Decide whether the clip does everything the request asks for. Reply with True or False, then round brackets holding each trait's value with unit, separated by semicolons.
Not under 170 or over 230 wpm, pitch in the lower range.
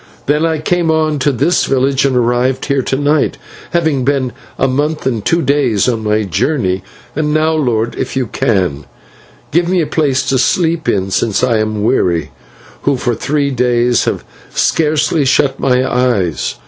True (175 wpm; 130 Hz)